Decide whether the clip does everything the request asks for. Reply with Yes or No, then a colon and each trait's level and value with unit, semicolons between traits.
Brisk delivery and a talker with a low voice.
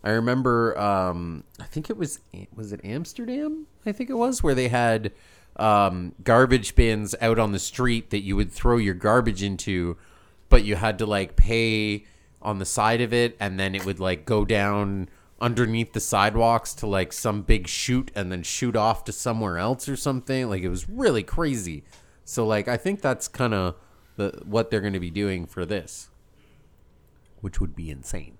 No: average, 190 wpm; low, 105 Hz